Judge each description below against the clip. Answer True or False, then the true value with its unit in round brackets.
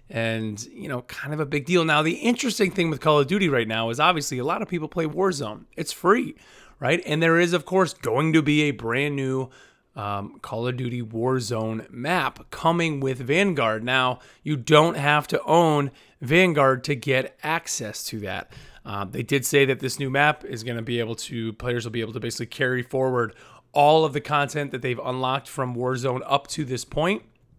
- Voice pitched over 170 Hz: False (135 Hz)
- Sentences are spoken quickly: True (210 wpm)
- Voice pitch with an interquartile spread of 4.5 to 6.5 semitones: False (4.0 semitones)